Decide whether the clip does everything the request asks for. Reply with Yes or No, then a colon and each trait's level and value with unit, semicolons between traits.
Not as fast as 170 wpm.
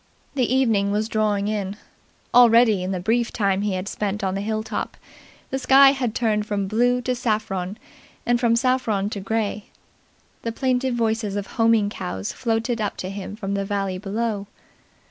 No: average, 175 wpm